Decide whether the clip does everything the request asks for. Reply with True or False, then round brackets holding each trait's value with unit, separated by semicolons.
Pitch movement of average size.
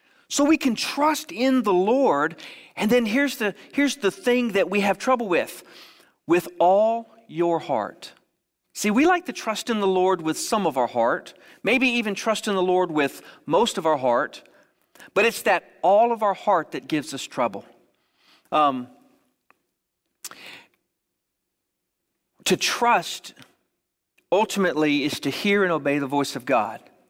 False (6.8 semitones)